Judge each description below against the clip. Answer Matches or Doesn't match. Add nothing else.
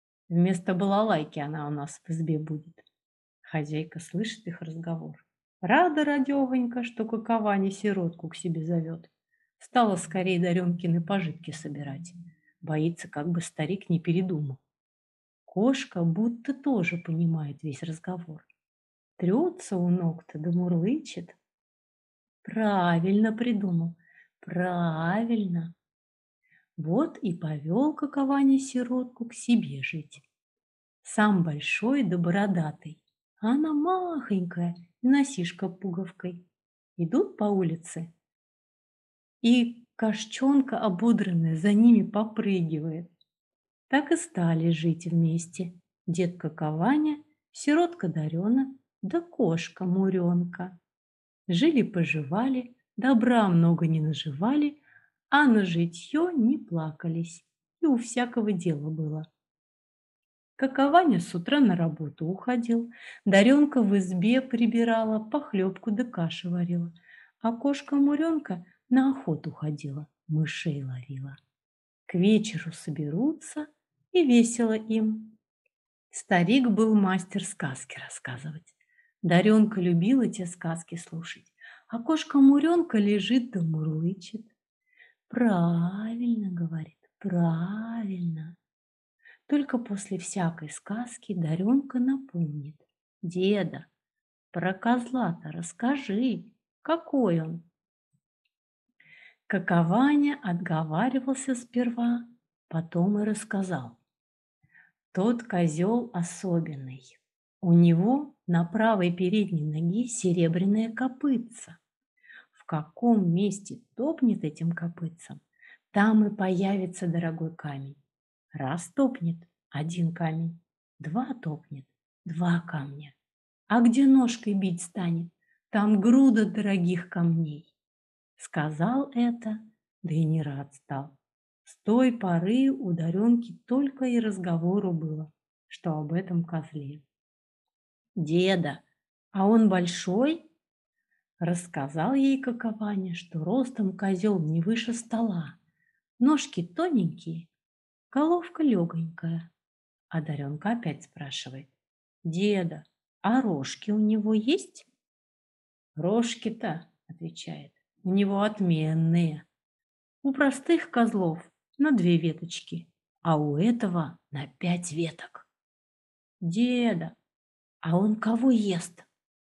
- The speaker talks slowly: Matches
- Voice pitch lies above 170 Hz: Matches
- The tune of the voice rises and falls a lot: Matches